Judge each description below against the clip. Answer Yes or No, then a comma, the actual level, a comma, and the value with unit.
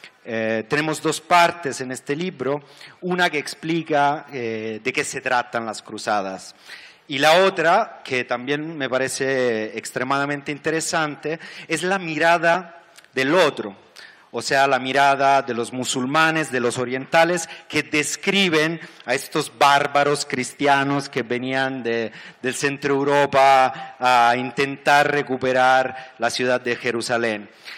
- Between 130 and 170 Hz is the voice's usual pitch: Yes, medium, 140 Hz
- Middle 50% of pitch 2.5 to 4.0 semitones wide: Yes, average, 3.4 semitones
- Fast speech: No, average, 130 wpm